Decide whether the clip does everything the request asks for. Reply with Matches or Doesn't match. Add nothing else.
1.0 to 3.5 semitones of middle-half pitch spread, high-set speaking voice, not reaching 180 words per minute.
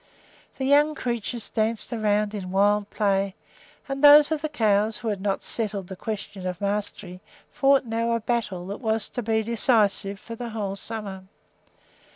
Matches